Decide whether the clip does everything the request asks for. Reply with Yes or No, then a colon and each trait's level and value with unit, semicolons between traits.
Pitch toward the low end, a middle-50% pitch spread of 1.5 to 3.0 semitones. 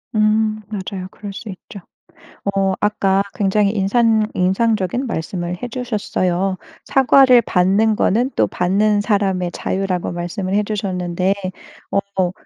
No: high, 200 Hz; narrow, 2.6 semitones